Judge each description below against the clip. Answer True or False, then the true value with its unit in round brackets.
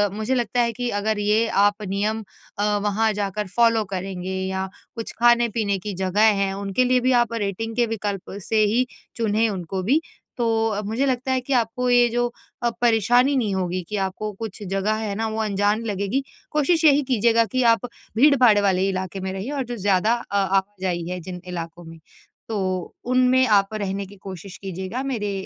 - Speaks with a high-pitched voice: True (210 Hz)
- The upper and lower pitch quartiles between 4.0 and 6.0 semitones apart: False (3.6 semitones)